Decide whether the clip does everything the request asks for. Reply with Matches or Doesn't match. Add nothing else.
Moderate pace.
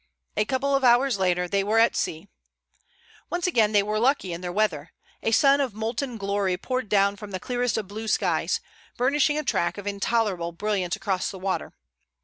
Matches